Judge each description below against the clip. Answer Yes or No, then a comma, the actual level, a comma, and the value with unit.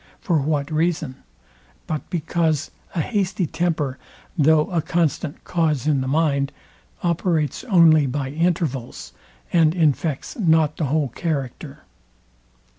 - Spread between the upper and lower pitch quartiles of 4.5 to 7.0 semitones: No, average, 3.1 semitones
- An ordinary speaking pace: No, slow, 115 wpm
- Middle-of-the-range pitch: Yes, medium, 155 Hz